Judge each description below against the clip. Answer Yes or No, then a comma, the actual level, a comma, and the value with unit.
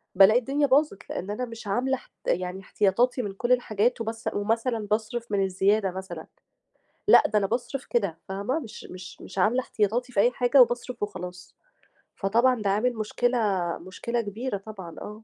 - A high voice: Yes, high, 215 Hz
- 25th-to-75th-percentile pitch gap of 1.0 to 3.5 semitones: No, average, 4.0 semitones